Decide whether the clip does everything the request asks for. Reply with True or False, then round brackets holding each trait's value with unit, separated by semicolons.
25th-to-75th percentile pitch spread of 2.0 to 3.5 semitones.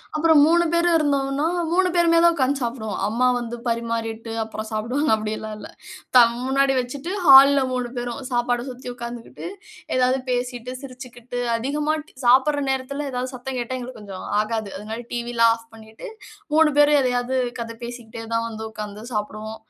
True (3.2 semitones)